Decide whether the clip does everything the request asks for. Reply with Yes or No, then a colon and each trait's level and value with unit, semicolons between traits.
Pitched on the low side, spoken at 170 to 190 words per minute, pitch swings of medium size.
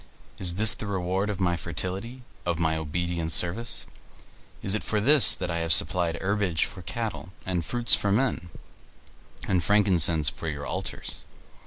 No: very low, 90 Hz; average, 160 wpm; average, 3.4 semitones